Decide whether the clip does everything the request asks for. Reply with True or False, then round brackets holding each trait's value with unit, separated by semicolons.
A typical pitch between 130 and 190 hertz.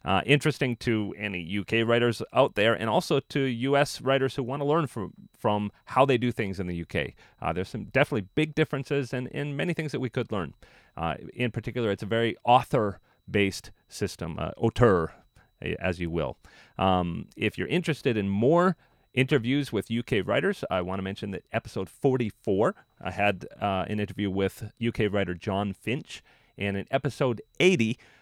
False (115 Hz)